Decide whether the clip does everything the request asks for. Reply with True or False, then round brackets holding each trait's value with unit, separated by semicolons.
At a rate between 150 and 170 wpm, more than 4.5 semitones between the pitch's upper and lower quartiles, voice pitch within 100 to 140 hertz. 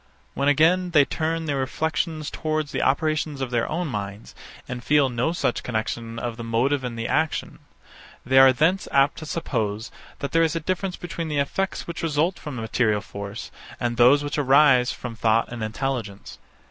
False (185 wpm; 5.0 semitones; 135 Hz)